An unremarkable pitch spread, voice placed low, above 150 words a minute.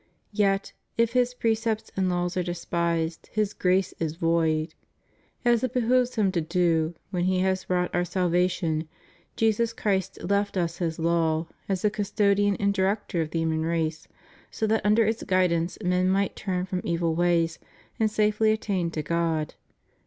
No: average, 3.7 semitones; medium, 185 Hz; average, 165 wpm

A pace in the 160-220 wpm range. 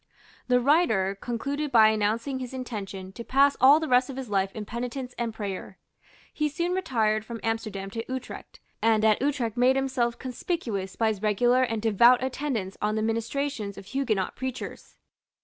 Yes: average, 170 wpm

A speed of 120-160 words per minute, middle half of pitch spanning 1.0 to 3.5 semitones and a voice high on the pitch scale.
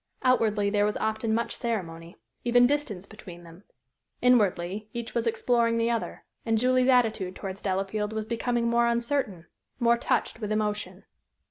Yes: average, 150 wpm; average, 2.7 semitones; high, 220 Hz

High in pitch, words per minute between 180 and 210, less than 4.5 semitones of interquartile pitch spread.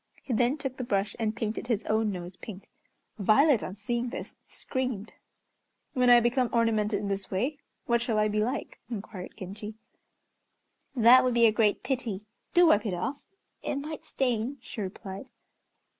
No: high, 225 Hz; average, 170 wpm; average, 3.4 semitones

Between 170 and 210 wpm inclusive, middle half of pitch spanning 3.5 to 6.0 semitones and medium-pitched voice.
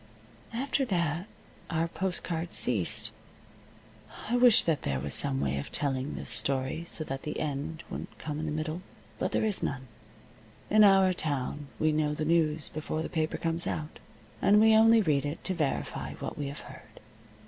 Yes: average, 180 wpm; average, 3.9 semitones; medium, 155 Hz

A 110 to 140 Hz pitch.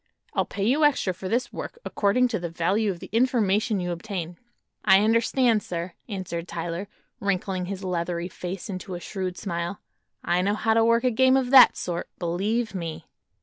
No: high, 195 Hz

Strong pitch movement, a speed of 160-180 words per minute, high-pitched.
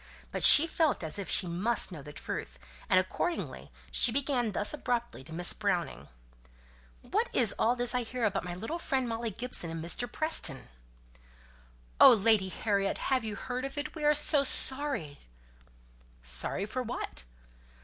Yes: wide, 6.2 semitones; average, 165 wpm; high, 230 Hz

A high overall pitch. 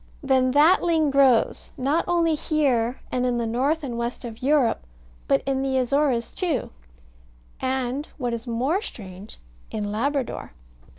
Yes: very high, 260 Hz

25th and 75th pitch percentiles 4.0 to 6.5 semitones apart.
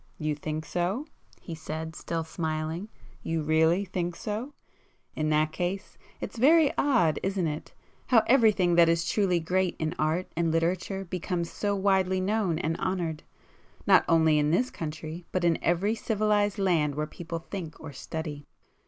No: average, 3.4 semitones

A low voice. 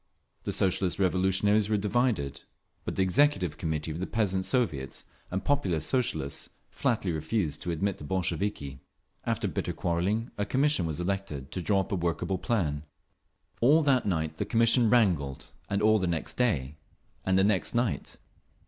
Yes: very low, 95 Hz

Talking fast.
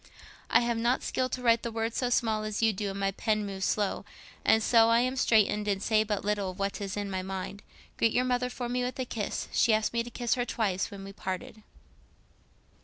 Yes: fast, 240 wpm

